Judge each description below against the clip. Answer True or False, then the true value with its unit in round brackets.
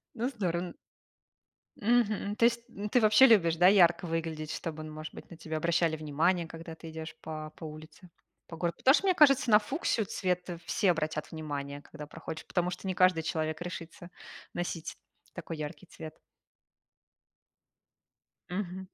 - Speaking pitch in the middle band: True (170 Hz)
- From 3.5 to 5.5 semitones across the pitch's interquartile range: True (4.0 semitones)